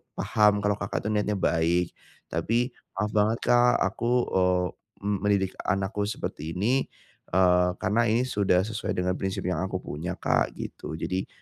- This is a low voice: Yes, low, 100 Hz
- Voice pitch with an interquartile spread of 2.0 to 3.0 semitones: Yes, average, 2.7 semitones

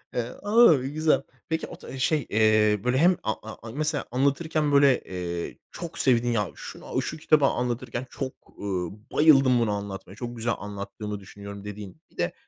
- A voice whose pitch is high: No, low, 120 Hz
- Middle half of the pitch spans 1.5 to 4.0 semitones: No, wide, 5.6 semitones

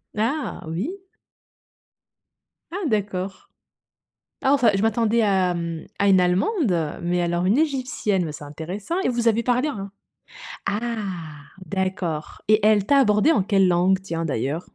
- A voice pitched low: No, high, 200 Hz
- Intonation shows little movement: No, average, 4.9 semitones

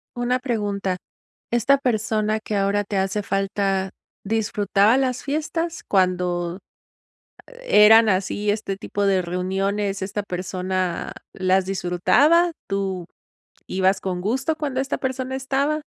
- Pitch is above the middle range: Yes, high, 200 Hz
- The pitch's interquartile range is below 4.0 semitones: No, average, 4.5 semitones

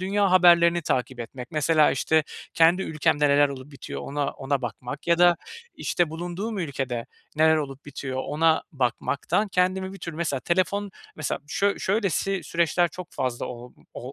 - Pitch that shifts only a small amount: No, average, 4.4 semitones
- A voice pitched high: No, medium, 160 Hz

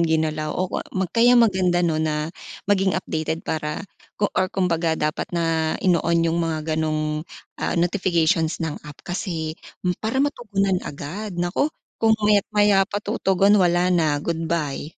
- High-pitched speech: No, medium, 170 Hz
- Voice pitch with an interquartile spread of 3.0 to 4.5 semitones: Yes, average, 3.4 semitones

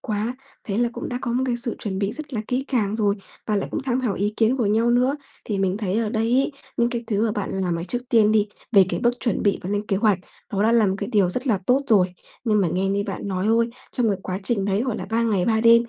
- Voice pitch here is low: No, high, 215 Hz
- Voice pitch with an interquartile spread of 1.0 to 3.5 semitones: Yes, average, 3.1 semitones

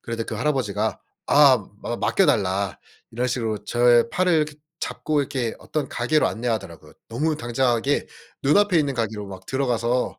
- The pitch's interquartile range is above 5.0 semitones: No, average, 4.4 semitones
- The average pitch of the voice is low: Yes, low, 120 Hz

